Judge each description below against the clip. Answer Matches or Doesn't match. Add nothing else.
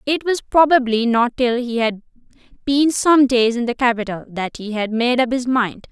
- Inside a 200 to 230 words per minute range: Matches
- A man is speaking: Doesn't match